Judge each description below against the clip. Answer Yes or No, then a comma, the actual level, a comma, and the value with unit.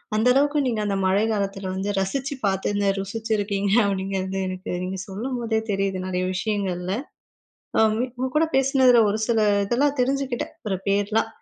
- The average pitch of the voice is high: Yes, high, 205 Hz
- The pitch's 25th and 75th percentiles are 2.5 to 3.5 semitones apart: No, average, 4.1 semitones